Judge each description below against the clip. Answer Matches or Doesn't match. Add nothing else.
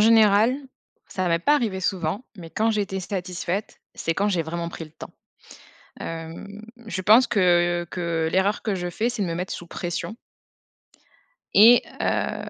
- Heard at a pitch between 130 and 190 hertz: Matches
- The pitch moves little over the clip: Doesn't match